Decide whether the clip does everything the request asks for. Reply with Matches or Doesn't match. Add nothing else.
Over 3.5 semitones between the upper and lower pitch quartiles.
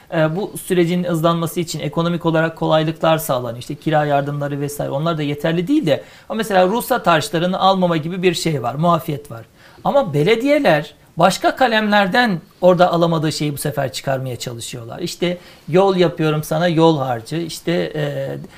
Doesn't match